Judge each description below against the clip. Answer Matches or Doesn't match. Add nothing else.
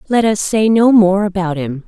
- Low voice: Doesn't match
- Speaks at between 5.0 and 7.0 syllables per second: Doesn't match